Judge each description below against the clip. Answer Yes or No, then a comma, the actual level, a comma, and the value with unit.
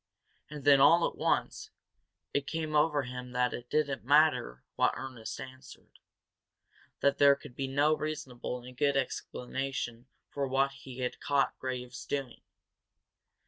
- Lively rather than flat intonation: No, narrow, 2.4 semitones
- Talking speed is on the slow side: No, average, 145 wpm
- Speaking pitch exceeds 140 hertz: No, low, 135 Hz